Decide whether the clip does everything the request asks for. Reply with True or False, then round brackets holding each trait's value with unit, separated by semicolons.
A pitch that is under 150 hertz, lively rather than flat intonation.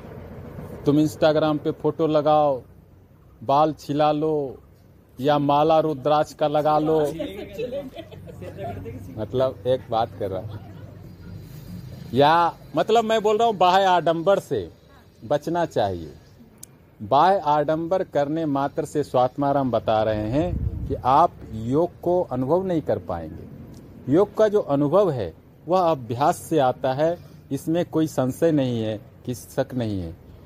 True (140 Hz; 5.9 semitones)